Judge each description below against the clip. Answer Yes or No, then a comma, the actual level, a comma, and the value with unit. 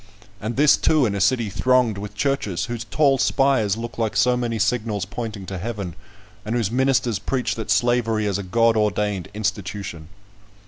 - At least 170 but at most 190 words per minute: Yes, average, 175 wpm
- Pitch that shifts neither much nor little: Yes, average, 3.2 semitones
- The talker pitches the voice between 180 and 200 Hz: No, low, 110 Hz